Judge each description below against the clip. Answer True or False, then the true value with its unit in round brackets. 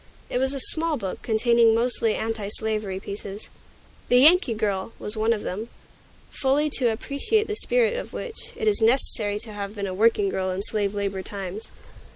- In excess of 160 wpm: True (180 wpm)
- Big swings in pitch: False (4.6 semitones)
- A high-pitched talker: True (220 Hz)